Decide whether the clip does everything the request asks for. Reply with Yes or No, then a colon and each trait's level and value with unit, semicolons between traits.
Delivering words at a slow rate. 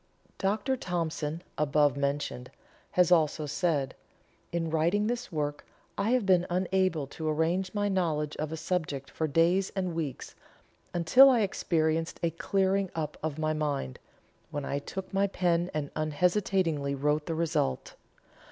No: average, 145 wpm